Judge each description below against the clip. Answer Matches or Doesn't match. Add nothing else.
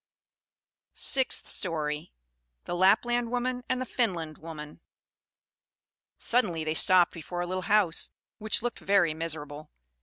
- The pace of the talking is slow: Matches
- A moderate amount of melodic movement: Doesn't match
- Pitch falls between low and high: Matches